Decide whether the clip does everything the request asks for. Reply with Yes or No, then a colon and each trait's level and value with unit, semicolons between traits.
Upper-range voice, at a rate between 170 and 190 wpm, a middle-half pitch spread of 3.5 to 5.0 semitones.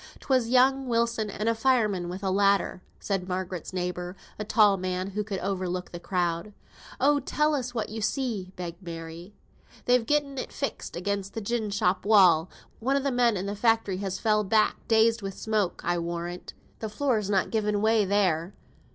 Yes: high, 205 Hz; average, 185 wpm; average, 3.8 semitones